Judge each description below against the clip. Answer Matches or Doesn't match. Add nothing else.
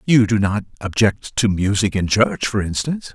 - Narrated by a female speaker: Doesn't match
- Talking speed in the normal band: Matches